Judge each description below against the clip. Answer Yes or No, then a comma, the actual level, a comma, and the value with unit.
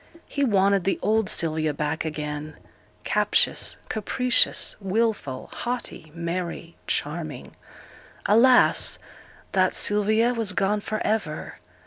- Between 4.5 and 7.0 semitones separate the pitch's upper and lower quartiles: Yes, wide, 5.6 semitones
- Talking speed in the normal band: No, slow, 100 wpm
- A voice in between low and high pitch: No, high, 195 Hz